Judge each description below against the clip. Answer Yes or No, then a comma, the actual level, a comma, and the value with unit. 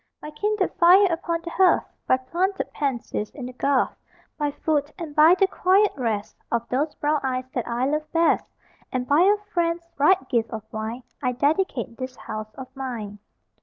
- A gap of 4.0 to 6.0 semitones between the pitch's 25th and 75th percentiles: Yes, average, 5.3 semitones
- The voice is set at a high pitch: Yes, very high, 285 Hz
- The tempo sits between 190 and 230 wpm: No, average, 180 wpm